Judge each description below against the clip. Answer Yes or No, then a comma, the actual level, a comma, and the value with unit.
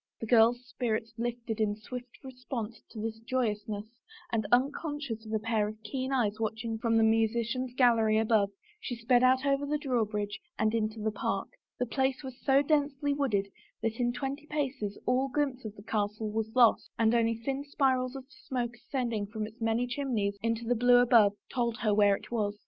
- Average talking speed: Yes, average, 190 wpm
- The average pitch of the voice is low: No, high, 230 Hz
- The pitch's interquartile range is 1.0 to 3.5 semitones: Yes, average, 2.9 semitones